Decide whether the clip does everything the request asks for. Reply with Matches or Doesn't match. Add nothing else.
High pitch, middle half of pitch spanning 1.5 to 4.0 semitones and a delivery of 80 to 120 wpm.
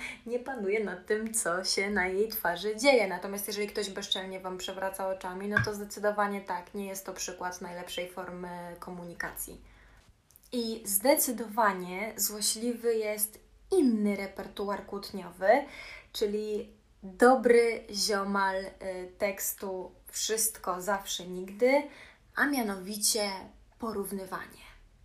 Matches